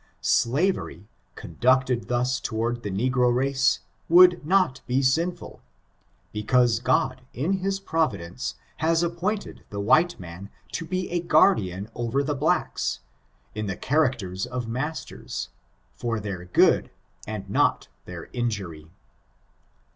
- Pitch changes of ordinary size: No, wide, 6.9 semitones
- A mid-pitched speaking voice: No, low, 125 Hz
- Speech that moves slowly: Yes, slow, 125 wpm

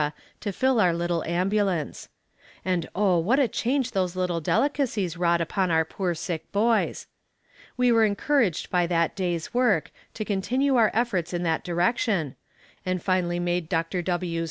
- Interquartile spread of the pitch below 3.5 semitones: No, average, 4.3 semitones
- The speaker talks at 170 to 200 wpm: No, average, 155 wpm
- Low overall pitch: No, medium, 185 Hz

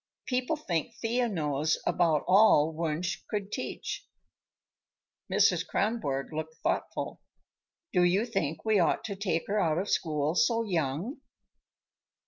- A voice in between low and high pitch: Yes, medium, 180 Hz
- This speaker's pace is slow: Yes, slow, 125 wpm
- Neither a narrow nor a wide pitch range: No, wide, 5.9 semitones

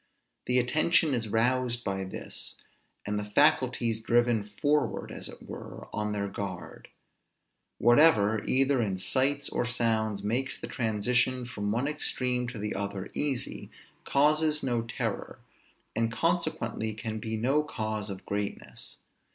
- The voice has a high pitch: No, low, 115 Hz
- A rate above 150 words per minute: No, slow, 135 wpm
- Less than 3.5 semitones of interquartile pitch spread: No, average, 3.8 semitones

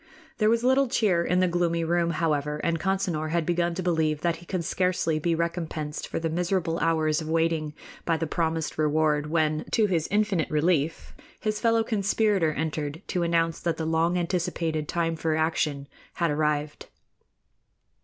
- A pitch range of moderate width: No, narrow, 2.2 semitones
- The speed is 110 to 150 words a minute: No, average, 170 wpm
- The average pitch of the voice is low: No, medium, 165 Hz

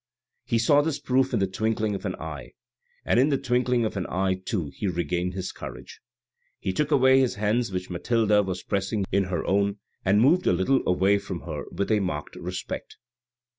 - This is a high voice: No, low, 100 Hz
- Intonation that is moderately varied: Yes, average, 4.4 semitones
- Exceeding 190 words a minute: Yes, average, 200 wpm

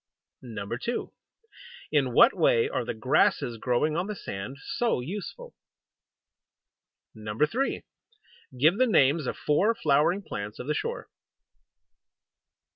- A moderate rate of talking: No, slow, 115 wpm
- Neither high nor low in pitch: Yes, medium, 170 Hz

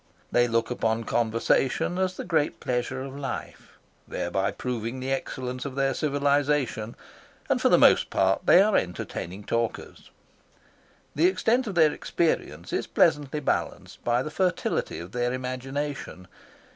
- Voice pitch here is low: Yes, low, 130 Hz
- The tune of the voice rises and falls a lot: No, average, 4.1 semitones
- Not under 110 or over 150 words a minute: Yes, average, 145 wpm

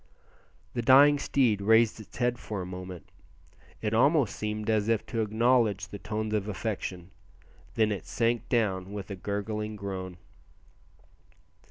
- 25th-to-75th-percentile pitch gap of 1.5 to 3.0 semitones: Yes, narrow, 2.5 semitones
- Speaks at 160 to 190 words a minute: No, average, 145 wpm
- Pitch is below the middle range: Yes, low, 105 Hz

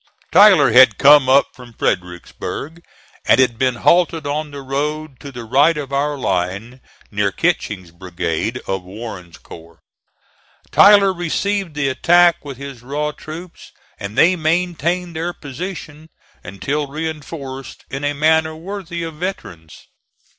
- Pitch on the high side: No, medium, 145 Hz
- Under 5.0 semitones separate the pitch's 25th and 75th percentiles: No, wide, 5.4 semitones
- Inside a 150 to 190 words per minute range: No, slow, 135 wpm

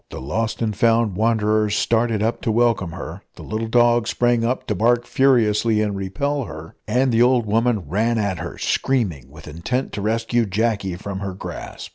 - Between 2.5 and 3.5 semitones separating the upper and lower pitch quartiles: Yes, average, 2.9 semitones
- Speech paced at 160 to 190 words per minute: Yes, average, 185 wpm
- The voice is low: Yes, low, 110 Hz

